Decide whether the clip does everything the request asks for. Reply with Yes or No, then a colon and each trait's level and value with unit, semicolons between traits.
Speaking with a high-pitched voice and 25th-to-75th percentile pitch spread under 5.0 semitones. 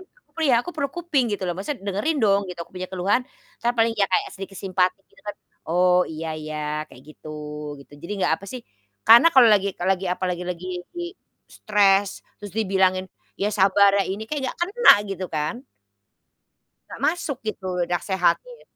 Yes: high, 195 Hz; average, 3.7 semitones